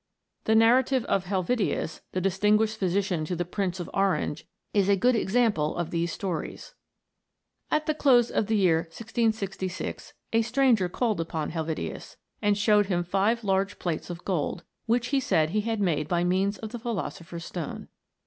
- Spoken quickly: No, average, 170 wpm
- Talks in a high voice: Yes, high, 195 Hz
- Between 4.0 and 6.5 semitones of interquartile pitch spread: Yes, average, 4.3 semitones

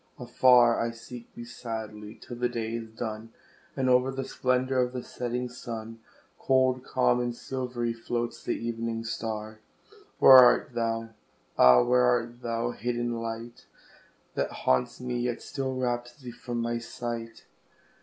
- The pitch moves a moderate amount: No, narrow, 1.5 semitones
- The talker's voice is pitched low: Yes, low, 120 Hz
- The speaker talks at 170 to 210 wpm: No, average, 155 wpm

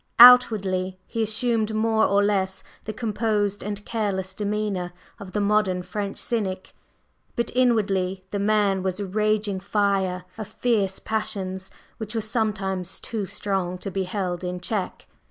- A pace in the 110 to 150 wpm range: Yes, average, 145 wpm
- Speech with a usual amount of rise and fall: No, narrow, 2.3 semitones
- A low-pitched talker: No, high, 205 Hz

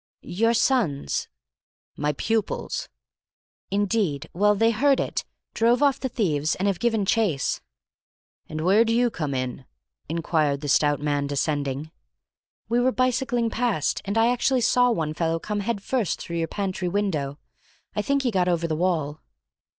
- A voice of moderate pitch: No, high, 195 Hz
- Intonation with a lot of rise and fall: Yes, wide, 6.9 semitones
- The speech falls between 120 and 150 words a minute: No, average, 160 wpm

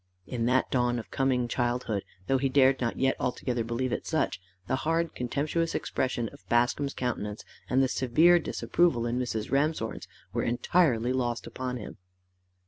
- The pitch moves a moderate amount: No, narrow, 2.3 semitones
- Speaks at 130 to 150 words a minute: No, average, 160 wpm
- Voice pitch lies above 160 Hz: No, low, 125 Hz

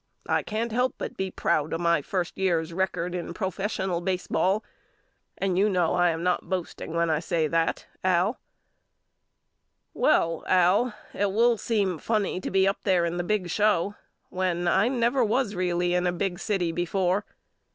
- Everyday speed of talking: Yes, average, 170 wpm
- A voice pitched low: No, medium, 185 Hz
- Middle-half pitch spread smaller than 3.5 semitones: Yes, average, 2.9 semitones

